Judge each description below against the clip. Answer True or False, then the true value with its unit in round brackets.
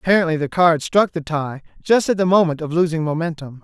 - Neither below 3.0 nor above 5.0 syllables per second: False (6.2 syllables/s)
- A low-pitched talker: False (165 Hz)